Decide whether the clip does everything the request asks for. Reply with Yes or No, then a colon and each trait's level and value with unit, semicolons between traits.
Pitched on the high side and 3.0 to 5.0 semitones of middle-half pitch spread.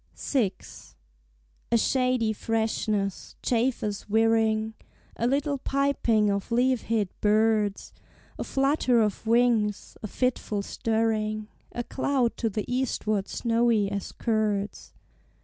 No: high, 225 Hz; narrow, 2.6 semitones